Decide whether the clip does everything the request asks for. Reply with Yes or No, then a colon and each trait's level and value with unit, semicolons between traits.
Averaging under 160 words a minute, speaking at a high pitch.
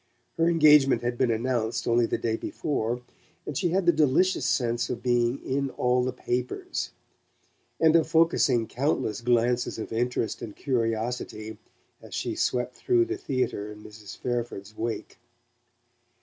No: average, 150 wpm; low, 125 Hz